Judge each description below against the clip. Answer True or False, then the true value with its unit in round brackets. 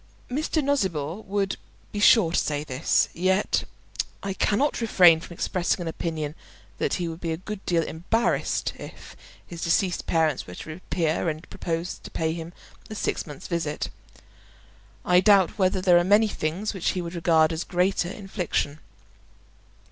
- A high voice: False (175 Hz)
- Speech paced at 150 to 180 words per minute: True (165 wpm)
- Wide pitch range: False (3.2 semitones)